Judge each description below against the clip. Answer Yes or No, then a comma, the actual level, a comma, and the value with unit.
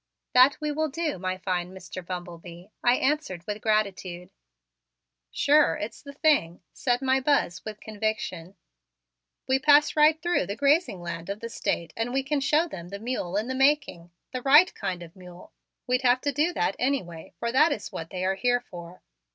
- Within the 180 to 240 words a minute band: Yes, average, 190 wpm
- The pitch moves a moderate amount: No, wide, 7.6 semitones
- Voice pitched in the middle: No, high, 225 Hz